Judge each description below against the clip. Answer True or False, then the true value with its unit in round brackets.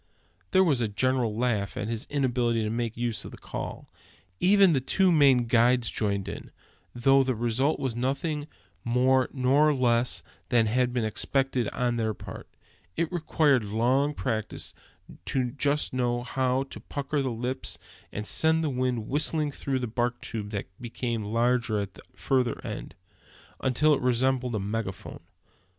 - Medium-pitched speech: False (125 Hz)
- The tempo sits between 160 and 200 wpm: True (165 wpm)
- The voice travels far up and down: False (2.8 semitones)